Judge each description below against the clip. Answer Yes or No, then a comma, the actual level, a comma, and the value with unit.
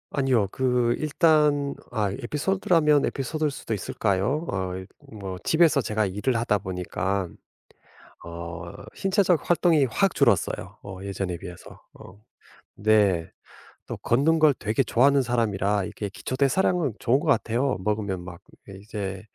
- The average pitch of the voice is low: Yes, low, 115 Hz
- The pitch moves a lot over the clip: Yes, wide, 6.7 semitones